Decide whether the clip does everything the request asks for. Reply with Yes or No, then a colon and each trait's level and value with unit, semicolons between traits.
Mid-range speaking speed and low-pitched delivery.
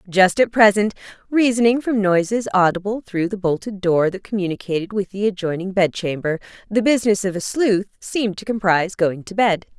No: average, 180 wpm; high, 200 Hz